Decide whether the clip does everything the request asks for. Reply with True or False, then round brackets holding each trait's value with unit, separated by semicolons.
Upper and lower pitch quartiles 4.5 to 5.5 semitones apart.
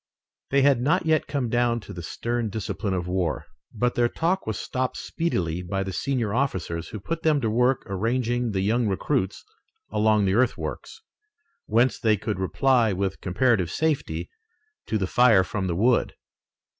True (5.1 semitones)